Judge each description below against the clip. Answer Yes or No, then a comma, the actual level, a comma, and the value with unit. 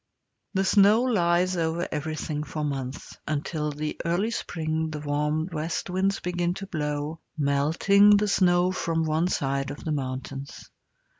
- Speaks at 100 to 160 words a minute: Yes, average, 150 wpm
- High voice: No, medium, 160 Hz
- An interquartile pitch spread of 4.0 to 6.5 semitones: No, average, 3.4 semitones